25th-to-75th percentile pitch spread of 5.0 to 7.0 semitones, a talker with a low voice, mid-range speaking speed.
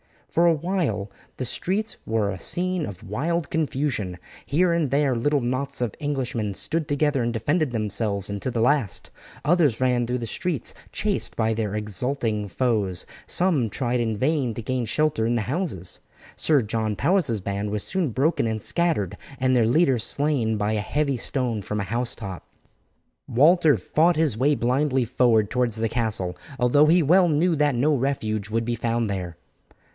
Yes: wide, 5.4 semitones; low, 125 Hz; average, 170 wpm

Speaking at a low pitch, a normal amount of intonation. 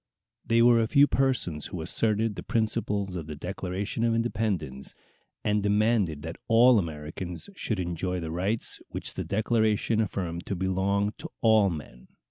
Yes: low, 100 Hz; average, 4.3 semitones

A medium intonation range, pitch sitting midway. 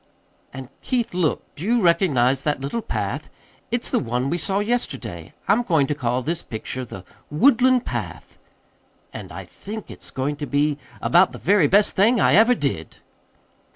No: wide, 7.9 semitones; medium, 155 Hz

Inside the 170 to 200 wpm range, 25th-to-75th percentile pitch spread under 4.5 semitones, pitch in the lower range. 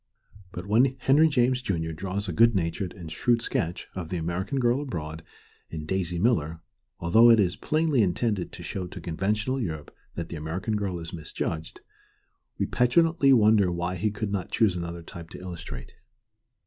No: average, 175 wpm; wide, 5.4 semitones; very low, 95 Hz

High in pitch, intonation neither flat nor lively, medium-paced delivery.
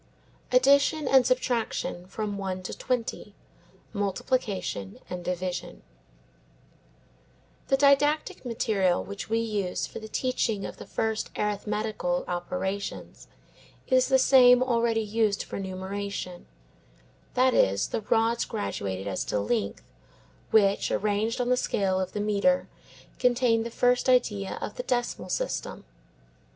No: high, 215 Hz; average, 4.6 semitones; slow, 125 wpm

